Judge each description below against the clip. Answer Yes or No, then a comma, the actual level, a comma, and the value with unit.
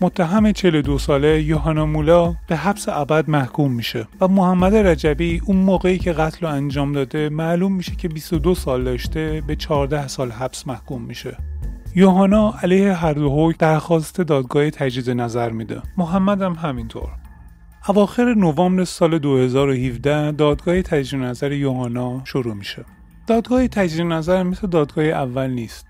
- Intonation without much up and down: No, average, 4.9 semitones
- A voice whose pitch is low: No, medium, 155 Hz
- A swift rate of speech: No, average, 140 wpm